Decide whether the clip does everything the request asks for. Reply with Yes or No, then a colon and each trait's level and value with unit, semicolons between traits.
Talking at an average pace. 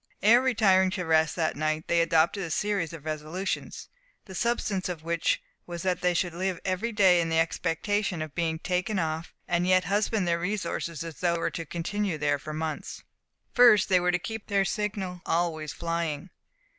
Yes: average, 190 wpm